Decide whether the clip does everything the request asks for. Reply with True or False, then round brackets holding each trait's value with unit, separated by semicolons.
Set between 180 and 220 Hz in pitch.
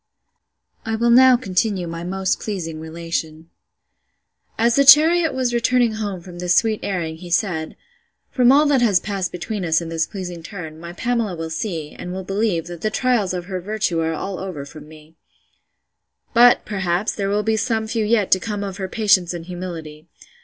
True (190 Hz)